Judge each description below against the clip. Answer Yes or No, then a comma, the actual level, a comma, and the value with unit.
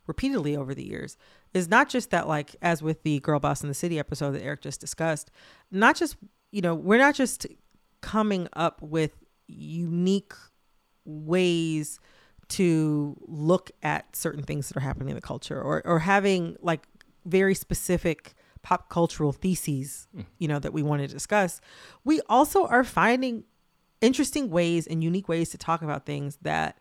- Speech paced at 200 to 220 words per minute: No, average, 170 wpm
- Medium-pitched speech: Yes, medium, 170 Hz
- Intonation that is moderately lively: Yes, average, 4.5 semitones